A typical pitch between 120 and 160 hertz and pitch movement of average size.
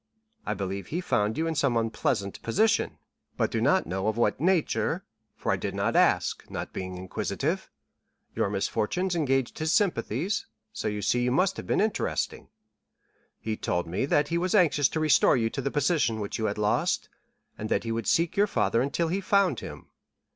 No: low, 135 Hz; wide, 8.2 semitones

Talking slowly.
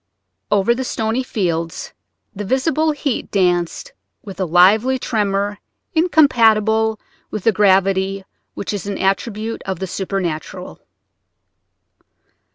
Yes: slow, 110 wpm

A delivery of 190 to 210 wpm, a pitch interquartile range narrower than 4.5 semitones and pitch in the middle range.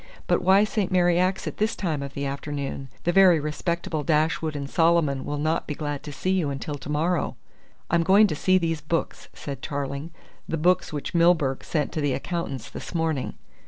Yes: average, 195 wpm; average, 3.4 semitones; medium, 155 Hz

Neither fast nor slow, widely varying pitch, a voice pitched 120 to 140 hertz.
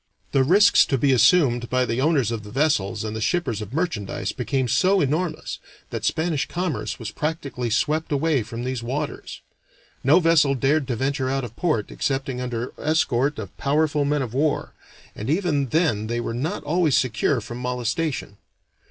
No: average, 170 wpm; average, 4.7 semitones; low, 135 Hz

